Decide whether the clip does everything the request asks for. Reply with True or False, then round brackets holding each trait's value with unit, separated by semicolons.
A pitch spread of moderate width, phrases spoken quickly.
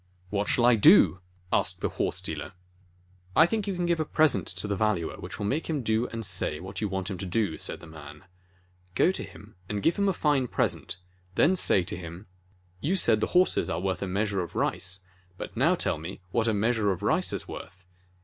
False (7.0 semitones; 235 wpm)